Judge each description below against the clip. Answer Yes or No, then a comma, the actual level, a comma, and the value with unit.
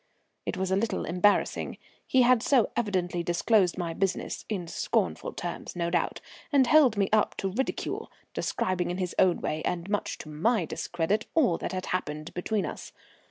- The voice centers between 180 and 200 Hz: Yes, medium, 185 Hz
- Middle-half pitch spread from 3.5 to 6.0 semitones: Yes, average, 3.9 semitones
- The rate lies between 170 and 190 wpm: Yes, average, 175 wpm